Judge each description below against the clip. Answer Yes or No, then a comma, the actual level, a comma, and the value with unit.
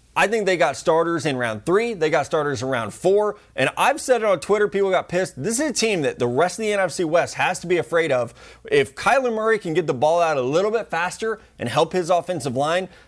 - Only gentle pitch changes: No, average, 5.0 semitones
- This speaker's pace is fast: Yes, fast, 255 wpm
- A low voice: No, medium, 180 Hz